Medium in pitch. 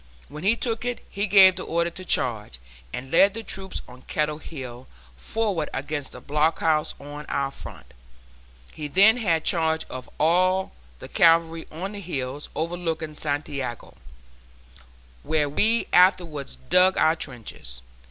Yes: medium, 160 Hz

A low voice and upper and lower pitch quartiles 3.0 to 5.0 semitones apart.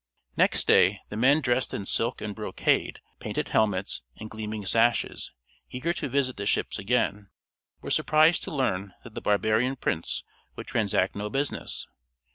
Yes: low, 110 Hz; average, 3.9 semitones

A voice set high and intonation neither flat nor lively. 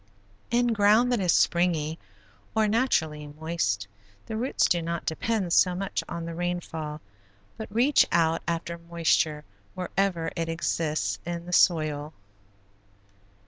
No: medium, 170 Hz; average, 3.6 semitones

